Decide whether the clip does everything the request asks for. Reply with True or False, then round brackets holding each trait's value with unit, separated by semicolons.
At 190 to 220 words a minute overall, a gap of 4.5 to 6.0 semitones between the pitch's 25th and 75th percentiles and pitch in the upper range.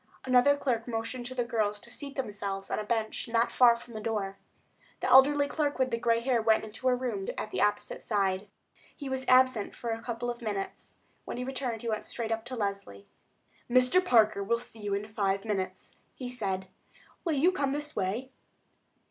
False (200 wpm; 3.5 semitones; 235 Hz)